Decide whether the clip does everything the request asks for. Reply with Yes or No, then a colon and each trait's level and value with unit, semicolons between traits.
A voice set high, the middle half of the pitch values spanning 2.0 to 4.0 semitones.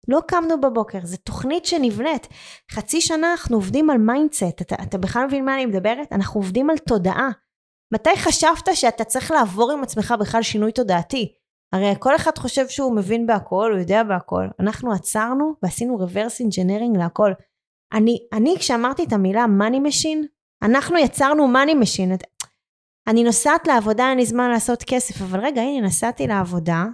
No: high, 235 Hz; average, 5.0 semitones